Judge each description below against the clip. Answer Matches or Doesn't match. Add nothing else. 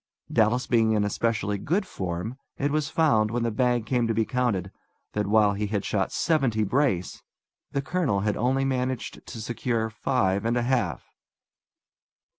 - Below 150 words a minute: Doesn't match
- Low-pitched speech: Matches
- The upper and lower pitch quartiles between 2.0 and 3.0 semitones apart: Doesn't match